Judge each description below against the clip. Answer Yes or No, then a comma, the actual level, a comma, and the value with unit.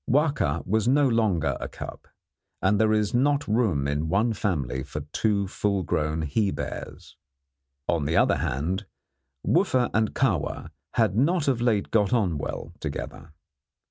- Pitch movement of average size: No, wide, 6.7 semitones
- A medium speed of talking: Yes, average, 150 wpm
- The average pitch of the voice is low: Yes, low, 105 Hz